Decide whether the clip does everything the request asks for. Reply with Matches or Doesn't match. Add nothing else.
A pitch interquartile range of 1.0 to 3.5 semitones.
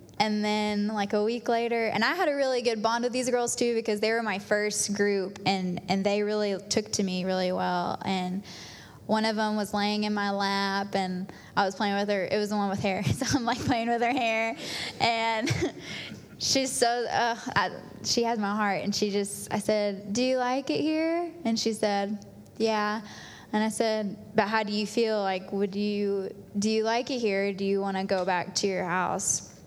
Matches